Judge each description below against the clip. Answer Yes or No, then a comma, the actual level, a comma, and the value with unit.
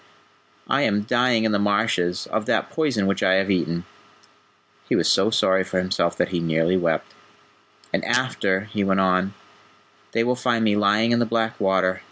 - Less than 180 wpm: No, average, 185 wpm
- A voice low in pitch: Yes, low, 100 Hz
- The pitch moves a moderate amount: Yes, average, 3.1 semitones